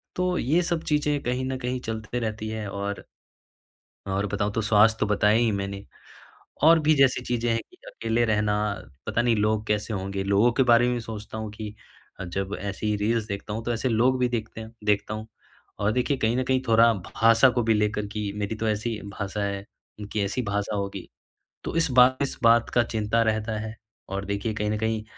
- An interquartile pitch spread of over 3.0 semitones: No, narrow, 2.4 semitones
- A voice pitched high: No, low, 110 Hz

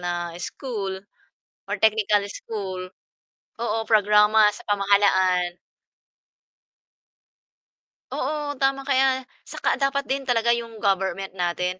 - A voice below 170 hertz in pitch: No, high, 210 Hz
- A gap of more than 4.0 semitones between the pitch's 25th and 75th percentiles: Yes, average, 5.2 semitones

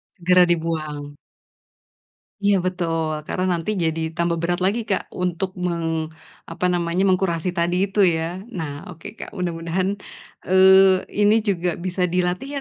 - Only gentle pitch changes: Yes, narrow, 2.1 semitones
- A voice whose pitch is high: No, medium, 180 Hz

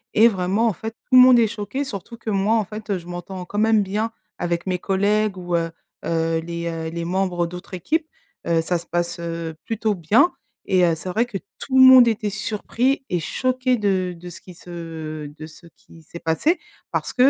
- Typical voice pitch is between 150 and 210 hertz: Yes, high, 190 Hz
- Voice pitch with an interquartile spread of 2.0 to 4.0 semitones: No, average, 4.7 semitones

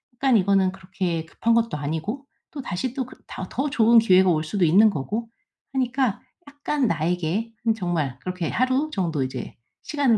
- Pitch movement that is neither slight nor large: No, wide, 6.1 semitones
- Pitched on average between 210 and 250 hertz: No, high, 200 Hz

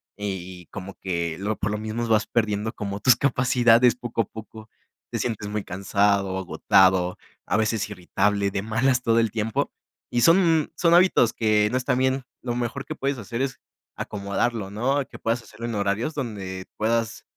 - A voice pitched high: No, low, 110 Hz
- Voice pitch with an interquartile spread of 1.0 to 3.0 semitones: No, average, 3.5 semitones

